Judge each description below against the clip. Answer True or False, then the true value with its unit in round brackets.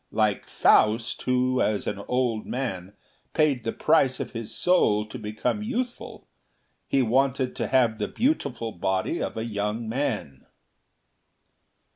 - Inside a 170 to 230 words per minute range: False (135 wpm)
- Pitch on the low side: True (115 Hz)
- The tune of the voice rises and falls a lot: False (3.8 semitones)